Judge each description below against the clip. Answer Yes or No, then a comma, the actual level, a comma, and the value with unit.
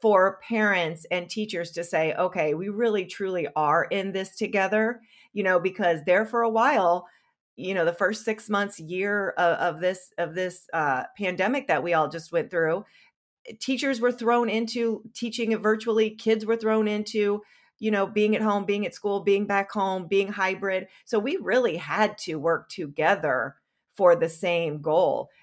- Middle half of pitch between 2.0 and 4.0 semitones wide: Yes, average, 3.6 semitones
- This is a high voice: Yes, high, 200 Hz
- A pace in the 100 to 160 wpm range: No, average, 175 wpm